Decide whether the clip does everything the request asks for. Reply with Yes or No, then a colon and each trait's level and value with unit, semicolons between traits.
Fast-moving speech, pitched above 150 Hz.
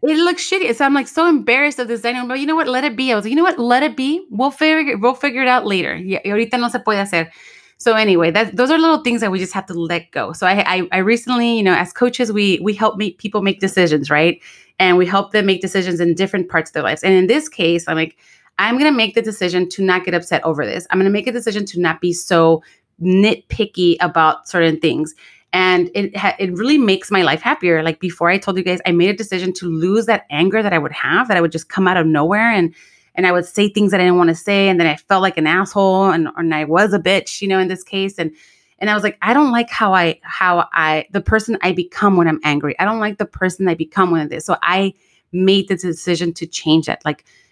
Yes: fast, 275 wpm; high, 190 Hz